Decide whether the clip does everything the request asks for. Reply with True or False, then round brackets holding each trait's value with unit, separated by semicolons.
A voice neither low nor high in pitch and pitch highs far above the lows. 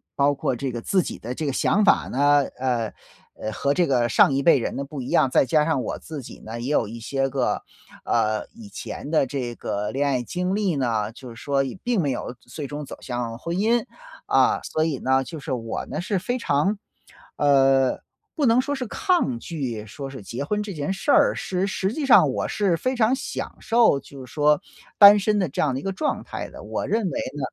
True (145 Hz; 7.0 semitones)